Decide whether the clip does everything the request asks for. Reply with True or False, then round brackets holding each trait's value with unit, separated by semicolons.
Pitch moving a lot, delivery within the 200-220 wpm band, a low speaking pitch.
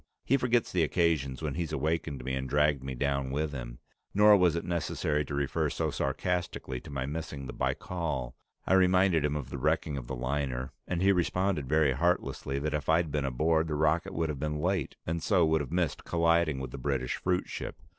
False (3.9 semitones; 205 wpm; 75 Hz)